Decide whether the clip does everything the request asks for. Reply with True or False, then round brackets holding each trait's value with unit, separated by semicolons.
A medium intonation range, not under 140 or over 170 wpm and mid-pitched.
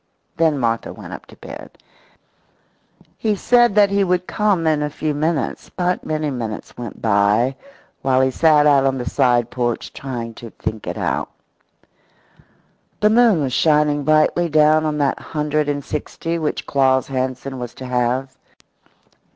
True (3.7 semitones; 160 wpm; 145 Hz)